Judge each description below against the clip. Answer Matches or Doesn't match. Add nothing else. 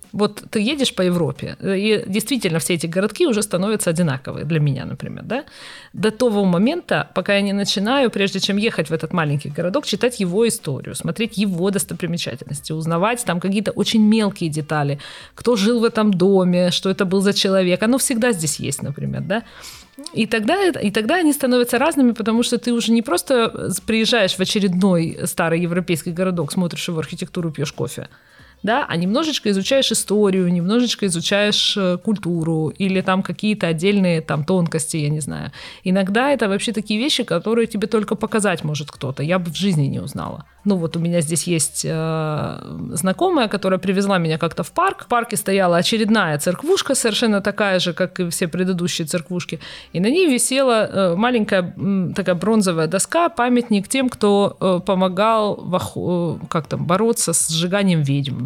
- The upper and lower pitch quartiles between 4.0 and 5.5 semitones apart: Matches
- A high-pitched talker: Matches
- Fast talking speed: Matches